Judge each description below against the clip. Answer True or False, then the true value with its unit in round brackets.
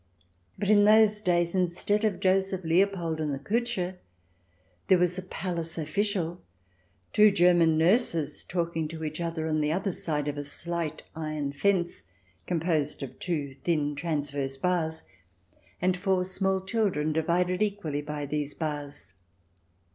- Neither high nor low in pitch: True (170 Hz)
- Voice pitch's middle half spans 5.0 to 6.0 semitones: False (3.7 semitones)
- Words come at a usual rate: True (145 wpm)